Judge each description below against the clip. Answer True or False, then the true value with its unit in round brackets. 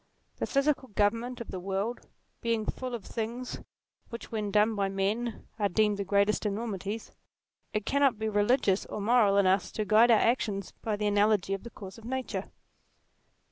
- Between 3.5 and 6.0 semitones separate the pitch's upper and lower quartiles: False (2.7 semitones)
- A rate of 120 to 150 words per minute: False (180 wpm)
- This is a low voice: False (215 Hz)